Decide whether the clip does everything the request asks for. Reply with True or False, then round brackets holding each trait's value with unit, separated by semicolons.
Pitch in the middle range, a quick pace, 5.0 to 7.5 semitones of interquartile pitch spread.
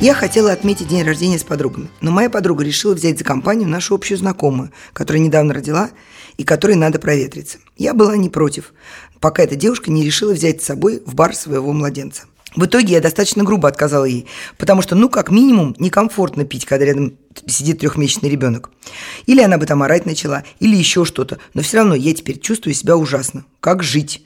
True (165 Hz; 195 wpm; 5.6 semitones)